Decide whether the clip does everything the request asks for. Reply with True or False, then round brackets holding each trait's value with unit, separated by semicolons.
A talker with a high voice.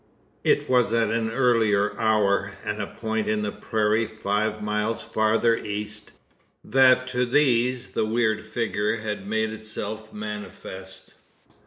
False (110 Hz)